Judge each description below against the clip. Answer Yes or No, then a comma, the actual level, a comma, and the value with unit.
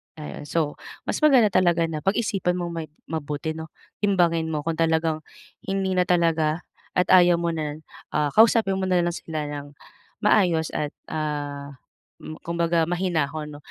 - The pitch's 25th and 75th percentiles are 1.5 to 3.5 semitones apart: Yes, average, 2.8 semitones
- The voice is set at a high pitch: No, medium, 165 Hz